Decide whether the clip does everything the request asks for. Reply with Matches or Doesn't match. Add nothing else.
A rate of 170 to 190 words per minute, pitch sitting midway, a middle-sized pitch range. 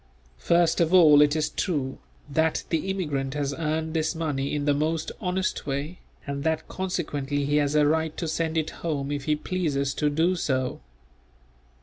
Doesn't match